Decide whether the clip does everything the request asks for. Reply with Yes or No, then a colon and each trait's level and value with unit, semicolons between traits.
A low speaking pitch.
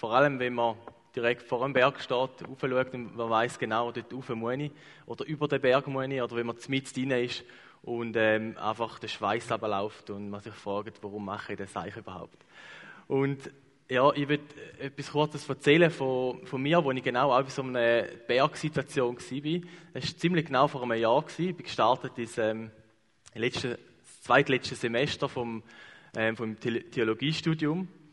Yes: low, 125 Hz